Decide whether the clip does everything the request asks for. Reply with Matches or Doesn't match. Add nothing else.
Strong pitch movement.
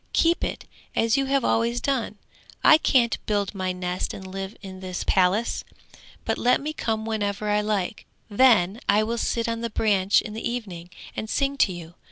Doesn't match